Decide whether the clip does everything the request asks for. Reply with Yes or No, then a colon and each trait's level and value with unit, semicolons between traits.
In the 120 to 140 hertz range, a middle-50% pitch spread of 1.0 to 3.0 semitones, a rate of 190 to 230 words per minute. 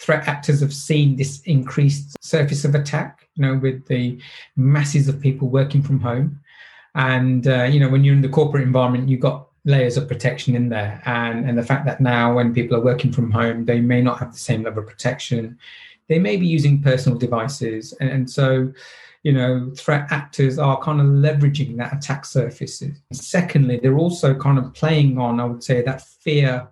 Yes: low, 135 Hz; narrow, 2.6 semitones; average, 200 wpm